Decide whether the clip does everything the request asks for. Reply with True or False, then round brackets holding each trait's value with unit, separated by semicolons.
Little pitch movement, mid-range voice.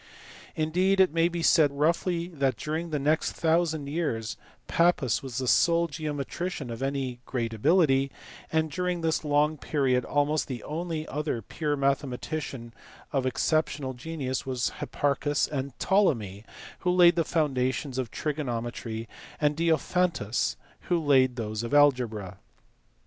False (4.0 semitones; 145 Hz)